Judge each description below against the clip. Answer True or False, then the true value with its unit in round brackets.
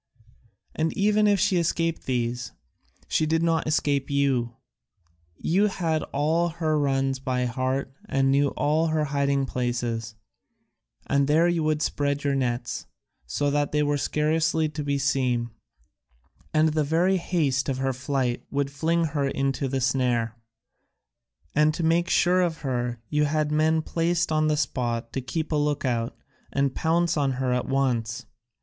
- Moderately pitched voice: True (145 Hz)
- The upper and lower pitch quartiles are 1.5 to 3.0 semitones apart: False (3.4 semitones)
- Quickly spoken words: False (160 wpm)